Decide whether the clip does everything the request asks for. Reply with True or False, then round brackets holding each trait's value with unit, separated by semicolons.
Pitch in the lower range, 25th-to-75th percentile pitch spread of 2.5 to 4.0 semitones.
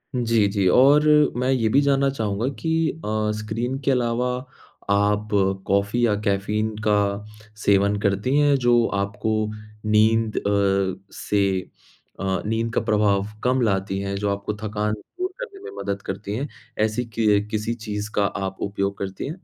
True (105 Hz; 3.1 semitones)